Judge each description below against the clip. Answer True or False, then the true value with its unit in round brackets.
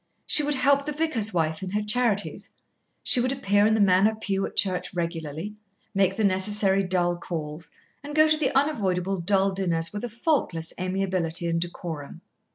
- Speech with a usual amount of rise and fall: True (4.2 semitones)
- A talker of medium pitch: False (195 Hz)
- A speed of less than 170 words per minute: False (175 wpm)